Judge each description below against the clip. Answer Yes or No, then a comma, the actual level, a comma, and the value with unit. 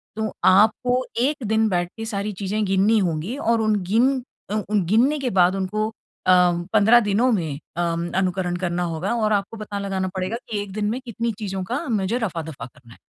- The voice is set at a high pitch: Yes, high, 205 Hz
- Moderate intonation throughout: Yes, average, 3.4 semitones